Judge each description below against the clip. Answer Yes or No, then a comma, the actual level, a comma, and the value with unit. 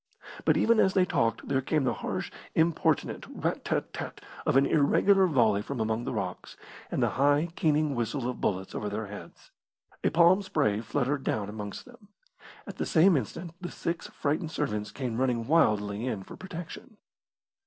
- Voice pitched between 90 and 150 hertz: Yes, medium, 140 Hz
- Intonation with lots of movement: Yes, wide, 7.2 semitones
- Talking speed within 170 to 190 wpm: Yes, average, 175 wpm